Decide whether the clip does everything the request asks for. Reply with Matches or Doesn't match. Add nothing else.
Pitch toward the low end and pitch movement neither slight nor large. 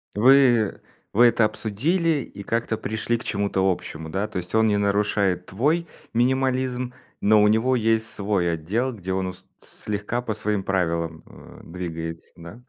Matches